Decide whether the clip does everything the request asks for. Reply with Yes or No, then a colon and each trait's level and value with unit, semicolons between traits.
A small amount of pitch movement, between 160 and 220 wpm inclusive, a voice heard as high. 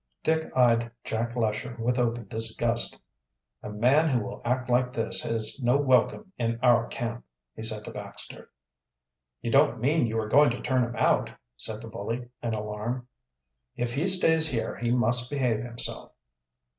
No: narrow, 2.0 semitones; average, 170 wpm; low, 120 Hz